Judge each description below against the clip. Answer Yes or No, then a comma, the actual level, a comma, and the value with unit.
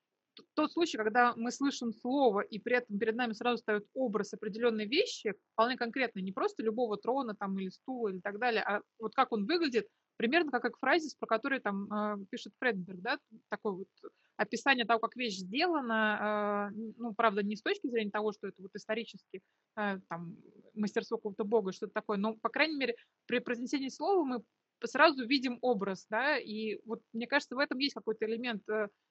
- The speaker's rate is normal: No, fast, 180 wpm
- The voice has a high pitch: Yes, high, 230 Hz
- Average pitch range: Yes, average, 3.5 semitones